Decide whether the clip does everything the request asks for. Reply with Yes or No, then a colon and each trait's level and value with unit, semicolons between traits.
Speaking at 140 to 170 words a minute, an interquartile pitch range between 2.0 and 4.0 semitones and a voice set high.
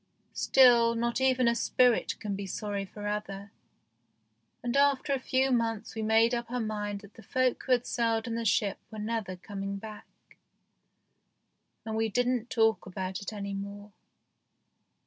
Yes: average, 165 wpm; average, 2.9 semitones; high, 225 Hz